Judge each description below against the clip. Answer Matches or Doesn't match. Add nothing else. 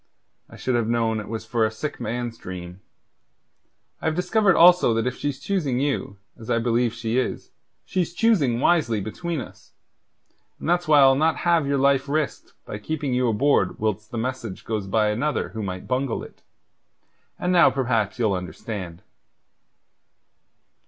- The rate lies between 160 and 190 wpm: Matches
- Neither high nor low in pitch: Doesn't match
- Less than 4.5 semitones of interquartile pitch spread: Doesn't match